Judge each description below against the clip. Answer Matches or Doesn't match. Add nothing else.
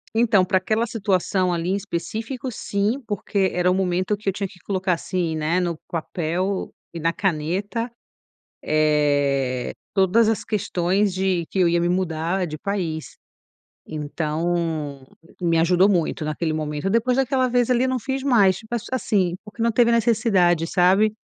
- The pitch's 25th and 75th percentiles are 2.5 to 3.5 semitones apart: Doesn't match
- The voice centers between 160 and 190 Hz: Matches